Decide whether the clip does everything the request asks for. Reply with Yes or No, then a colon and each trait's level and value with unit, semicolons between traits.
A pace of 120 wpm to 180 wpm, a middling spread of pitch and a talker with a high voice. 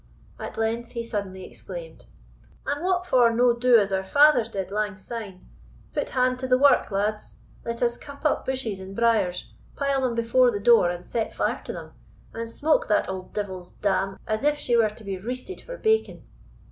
No: average, 195 wpm; average, 4.2 semitones; high, 230 Hz